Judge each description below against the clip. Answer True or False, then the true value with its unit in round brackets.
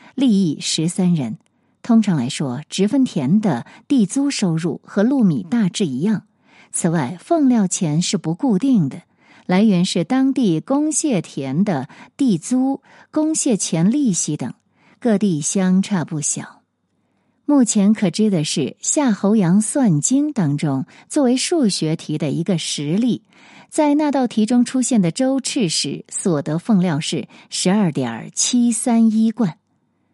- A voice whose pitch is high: True (205 Hz)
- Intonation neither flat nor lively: False (6.1 semitones)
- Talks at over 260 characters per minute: False (205 characters per minute)